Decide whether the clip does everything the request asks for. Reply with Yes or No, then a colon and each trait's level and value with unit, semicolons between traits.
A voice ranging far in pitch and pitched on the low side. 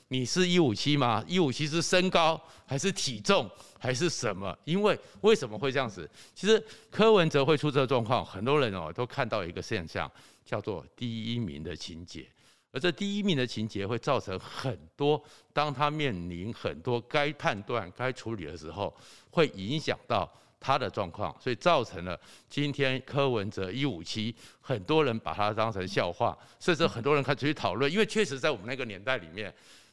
Yes: wide, 5.9 semitones; low, 130 Hz